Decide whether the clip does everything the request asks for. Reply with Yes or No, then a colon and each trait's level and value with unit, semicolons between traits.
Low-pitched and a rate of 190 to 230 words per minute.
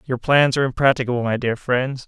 Yes: low, 125 Hz; average, 200 wpm